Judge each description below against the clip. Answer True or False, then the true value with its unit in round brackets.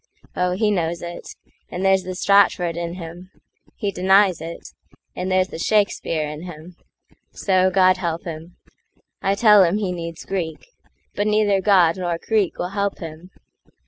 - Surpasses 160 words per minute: False (145 wpm)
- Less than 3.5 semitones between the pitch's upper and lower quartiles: True (2.6 semitones)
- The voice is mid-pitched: True (180 Hz)